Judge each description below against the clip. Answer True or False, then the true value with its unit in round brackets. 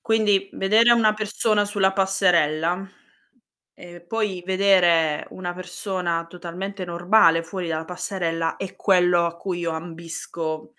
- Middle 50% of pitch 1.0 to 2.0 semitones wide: False (2.6 semitones)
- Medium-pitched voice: True (180 Hz)